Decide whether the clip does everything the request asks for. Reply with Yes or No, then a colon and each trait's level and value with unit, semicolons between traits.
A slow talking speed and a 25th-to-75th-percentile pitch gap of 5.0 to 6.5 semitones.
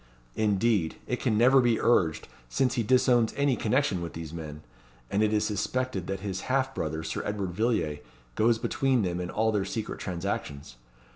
No: average, 175 wpm; wide, 5.4 semitones